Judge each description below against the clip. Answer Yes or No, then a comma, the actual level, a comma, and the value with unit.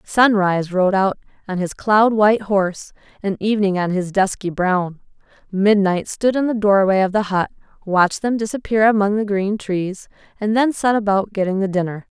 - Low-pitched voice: No, high, 200 Hz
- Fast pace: No, average, 180 wpm